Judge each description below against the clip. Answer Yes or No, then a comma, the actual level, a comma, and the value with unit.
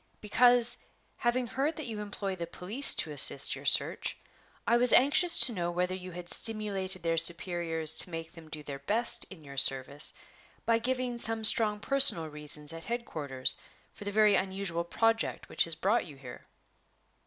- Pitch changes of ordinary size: No, wide, 5.9 semitones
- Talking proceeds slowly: No, average, 175 wpm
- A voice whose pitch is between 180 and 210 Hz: Yes, high, 190 Hz